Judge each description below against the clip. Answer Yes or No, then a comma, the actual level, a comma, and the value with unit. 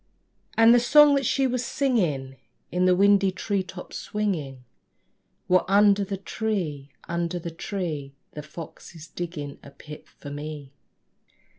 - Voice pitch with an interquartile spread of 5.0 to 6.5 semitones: Yes, wide, 5.5 semitones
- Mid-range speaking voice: Yes, medium, 180 Hz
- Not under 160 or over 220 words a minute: No, average, 145 wpm